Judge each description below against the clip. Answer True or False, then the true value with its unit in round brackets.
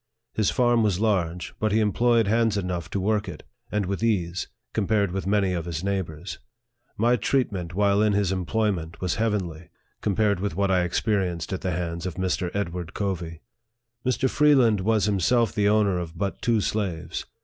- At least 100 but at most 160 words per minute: False (175 wpm)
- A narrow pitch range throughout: False (3.3 semitones)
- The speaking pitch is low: True (100 Hz)